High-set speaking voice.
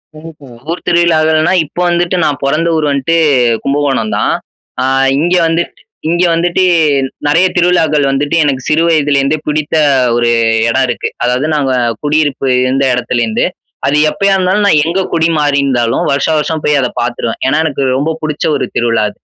No: medium, 150 Hz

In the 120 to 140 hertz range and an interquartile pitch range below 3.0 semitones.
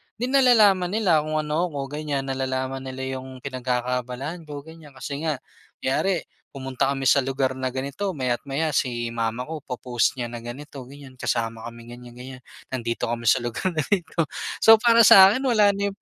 No: low, 135 Hz; average, 4.3 semitones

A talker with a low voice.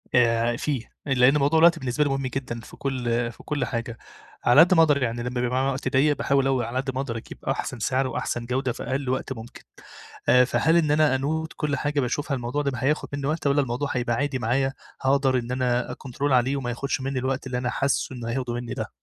Yes: low, 130 Hz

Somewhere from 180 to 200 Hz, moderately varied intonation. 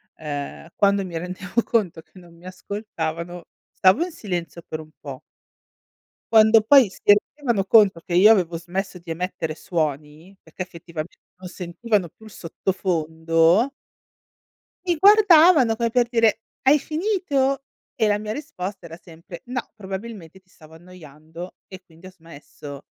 Yes: medium, 185 Hz; average, 5.0 semitones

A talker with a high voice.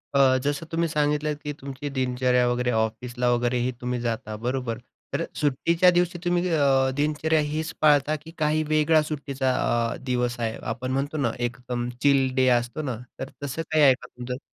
No: low, 135 Hz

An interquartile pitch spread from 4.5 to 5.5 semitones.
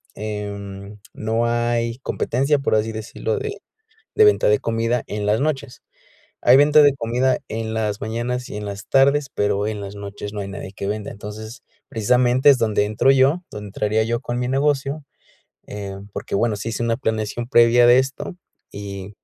No: average, 3.5 semitones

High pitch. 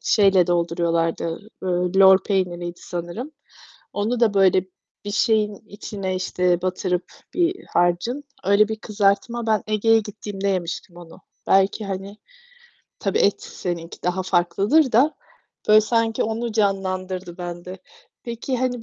Yes: high, 195 Hz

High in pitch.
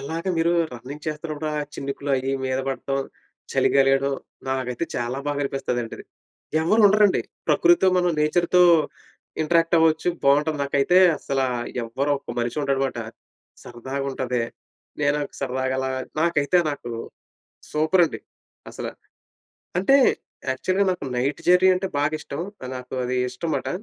No: medium, 140 Hz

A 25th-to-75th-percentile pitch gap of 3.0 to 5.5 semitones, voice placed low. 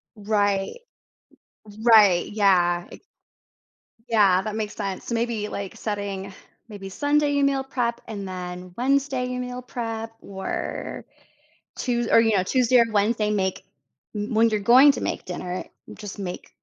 No: average, 3.6 semitones; high, 215 Hz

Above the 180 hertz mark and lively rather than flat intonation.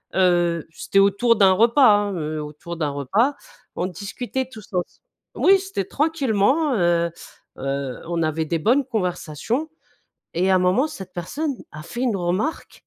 Yes: high, 190 Hz; wide, 6.4 semitones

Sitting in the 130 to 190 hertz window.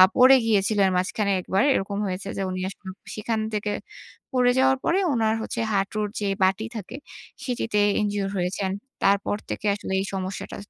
No: high, 205 Hz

